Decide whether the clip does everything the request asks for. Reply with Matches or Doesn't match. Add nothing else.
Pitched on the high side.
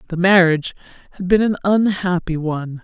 Doesn't match